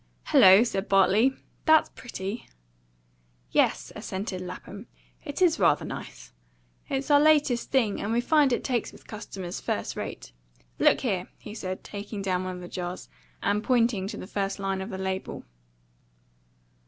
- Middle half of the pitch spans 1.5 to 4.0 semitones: No, average, 4.4 semitones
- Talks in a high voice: Yes, high, 200 Hz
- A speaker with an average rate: Yes, average, 155 wpm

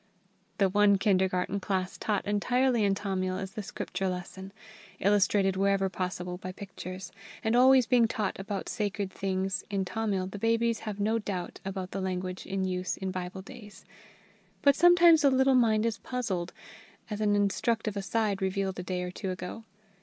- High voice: Yes, high, 195 Hz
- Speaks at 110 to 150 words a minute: No, average, 170 wpm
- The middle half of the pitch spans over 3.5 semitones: No, narrow, 2.6 semitones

